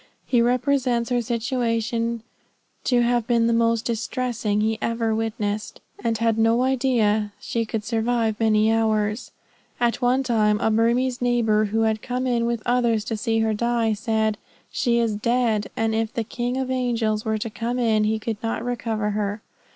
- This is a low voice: No, high, 230 Hz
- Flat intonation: Yes, narrow, 1.8 semitones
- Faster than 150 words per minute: Yes, average, 175 wpm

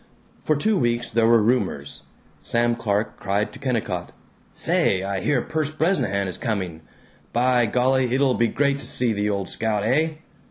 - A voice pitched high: No, low, 120 Hz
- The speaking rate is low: No, average, 165 wpm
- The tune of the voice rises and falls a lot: No, average, 4.3 semitones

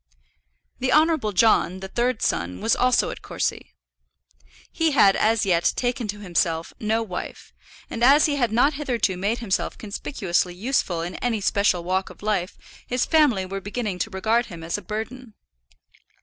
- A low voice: No, high, 215 Hz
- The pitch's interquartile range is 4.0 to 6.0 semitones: Yes, average, 4.7 semitones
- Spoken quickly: No, average, 165 wpm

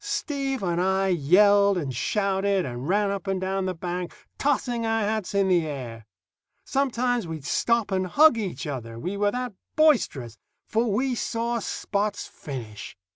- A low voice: No, high, 200 Hz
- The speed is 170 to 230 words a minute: No, average, 160 wpm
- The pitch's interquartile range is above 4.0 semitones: Yes, average, 5.1 semitones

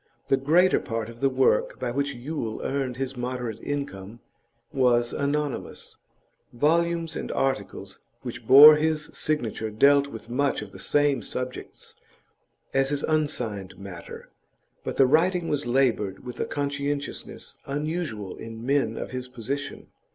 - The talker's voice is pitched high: No, low, 135 Hz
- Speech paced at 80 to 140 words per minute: Yes, slow, 135 wpm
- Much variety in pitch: No, average, 3.7 semitones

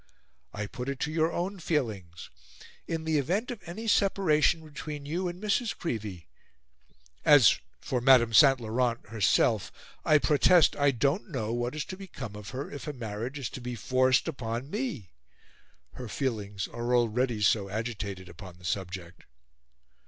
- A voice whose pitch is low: Yes, low, 130 Hz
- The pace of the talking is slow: No, average, 160 wpm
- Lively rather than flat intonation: Yes, wide, 6.1 semitones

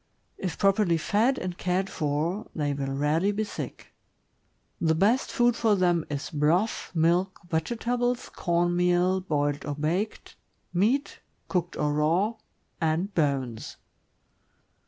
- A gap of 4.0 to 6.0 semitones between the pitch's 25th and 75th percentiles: Yes, average, 4.8 semitones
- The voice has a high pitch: No, medium, 175 Hz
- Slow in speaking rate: Yes, slow, 130 wpm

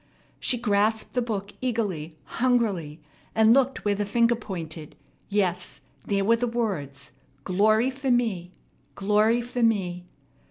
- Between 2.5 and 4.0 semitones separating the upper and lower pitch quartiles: No, average, 4.4 semitones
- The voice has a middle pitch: No, high, 210 Hz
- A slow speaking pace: Yes, slow, 130 wpm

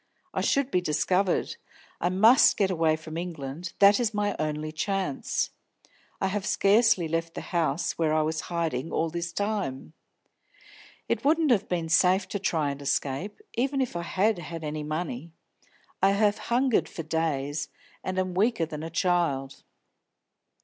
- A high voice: No, medium, 170 Hz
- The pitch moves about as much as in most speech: Yes, average, 4.2 semitones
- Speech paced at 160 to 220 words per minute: Yes, average, 165 wpm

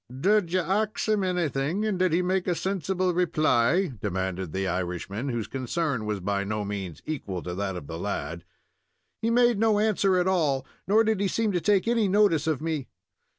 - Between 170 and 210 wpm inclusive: Yes, average, 195 wpm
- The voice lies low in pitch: No, medium, 165 Hz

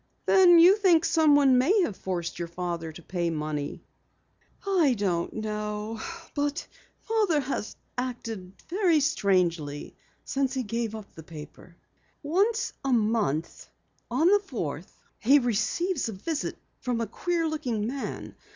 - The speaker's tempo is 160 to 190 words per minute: No, slow, 135 wpm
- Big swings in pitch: Yes, wide, 9.0 semitones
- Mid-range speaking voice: No, high, 235 Hz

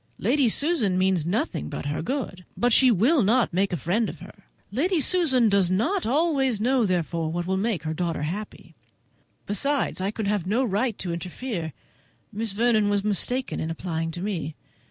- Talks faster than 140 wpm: Yes, average, 180 wpm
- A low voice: No, high, 205 Hz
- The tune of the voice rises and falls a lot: Yes, wide, 5.9 semitones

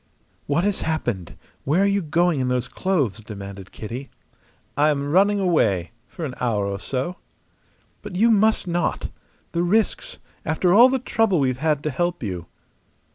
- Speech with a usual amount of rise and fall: No, wide, 7.1 semitones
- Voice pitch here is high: No, medium, 155 Hz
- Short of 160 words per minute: No, average, 165 wpm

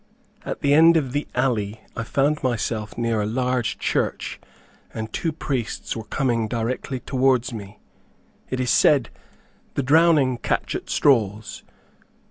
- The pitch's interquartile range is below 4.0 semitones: Yes, average, 3.6 semitones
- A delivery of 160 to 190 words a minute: No, average, 140 wpm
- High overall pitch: No, low, 125 Hz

